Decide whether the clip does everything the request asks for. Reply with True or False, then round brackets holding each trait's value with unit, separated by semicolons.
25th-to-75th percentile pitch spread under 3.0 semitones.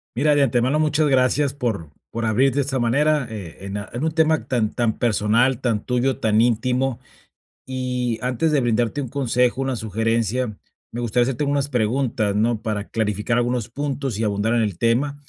False (3.3 semitones)